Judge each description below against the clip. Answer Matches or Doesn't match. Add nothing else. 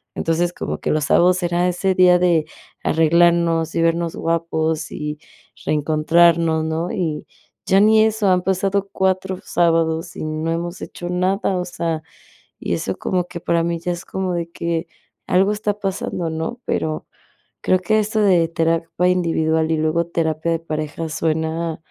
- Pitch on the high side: Doesn't match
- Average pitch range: Doesn't match